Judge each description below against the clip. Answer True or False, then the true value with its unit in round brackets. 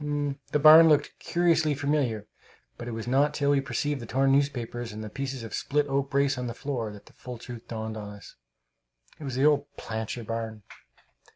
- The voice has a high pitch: False (135 Hz)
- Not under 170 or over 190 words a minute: False (200 wpm)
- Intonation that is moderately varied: True (4.1 semitones)